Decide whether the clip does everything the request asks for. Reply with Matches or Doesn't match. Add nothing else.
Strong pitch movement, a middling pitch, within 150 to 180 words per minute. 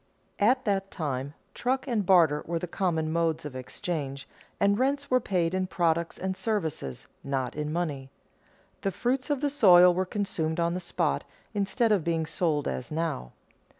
Doesn't match